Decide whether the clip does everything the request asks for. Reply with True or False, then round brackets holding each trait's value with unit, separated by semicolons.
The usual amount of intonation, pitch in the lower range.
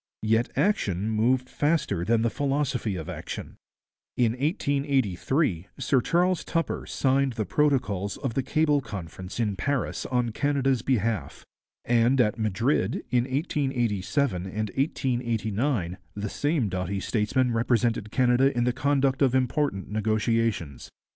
True (4.4 semitones; 120 Hz)